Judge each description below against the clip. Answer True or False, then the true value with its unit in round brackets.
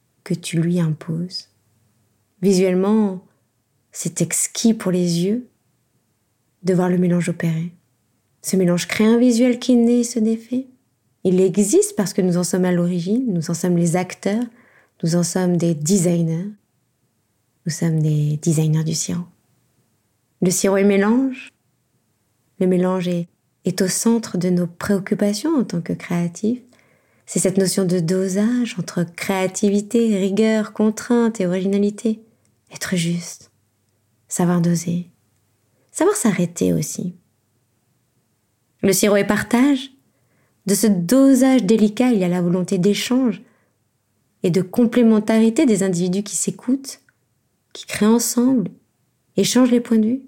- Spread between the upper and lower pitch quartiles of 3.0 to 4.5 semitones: False (5.0 semitones)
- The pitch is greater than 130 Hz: True (185 Hz)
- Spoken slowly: True (135 wpm)